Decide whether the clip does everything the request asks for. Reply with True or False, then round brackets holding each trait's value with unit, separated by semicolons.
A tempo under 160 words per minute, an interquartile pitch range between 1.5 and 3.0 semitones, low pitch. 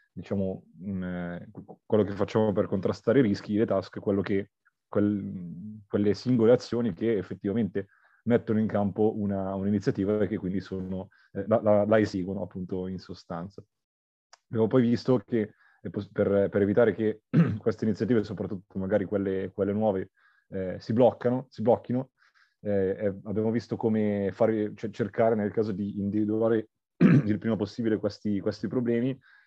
True (140 wpm; 2.4 semitones; 105 Hz)